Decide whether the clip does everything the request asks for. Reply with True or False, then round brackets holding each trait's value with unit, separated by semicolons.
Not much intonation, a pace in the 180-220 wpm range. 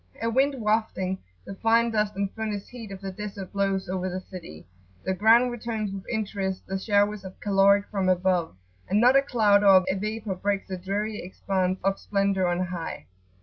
True (2.3 semitones; 190 wpm)